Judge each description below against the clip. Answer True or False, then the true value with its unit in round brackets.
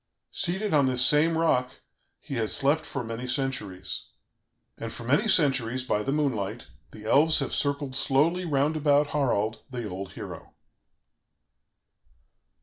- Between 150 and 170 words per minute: False (140 wpm)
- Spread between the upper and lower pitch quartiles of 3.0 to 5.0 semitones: True (4.5 semitones)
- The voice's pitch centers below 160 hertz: True (135 Hz)